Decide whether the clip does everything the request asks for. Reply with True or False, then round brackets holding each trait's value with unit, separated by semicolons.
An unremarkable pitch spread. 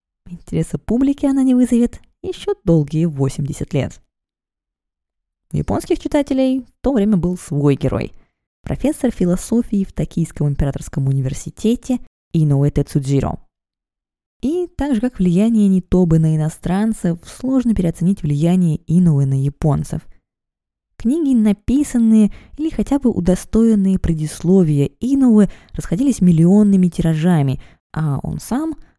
False (7.6 semitones)